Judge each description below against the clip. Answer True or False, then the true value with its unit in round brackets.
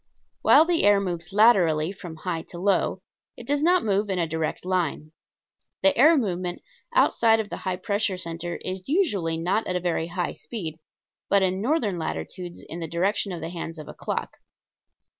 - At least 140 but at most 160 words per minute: False (185 wpm)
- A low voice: False (185 Hz)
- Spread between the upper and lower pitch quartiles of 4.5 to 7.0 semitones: False (3.8 semitones)